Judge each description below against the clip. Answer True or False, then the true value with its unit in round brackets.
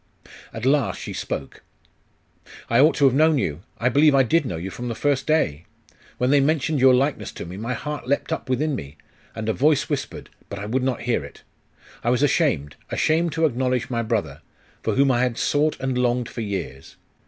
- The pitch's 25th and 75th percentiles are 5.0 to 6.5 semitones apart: False (4.2 semitones)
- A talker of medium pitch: False (130 Hz)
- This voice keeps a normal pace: False (210 wpm)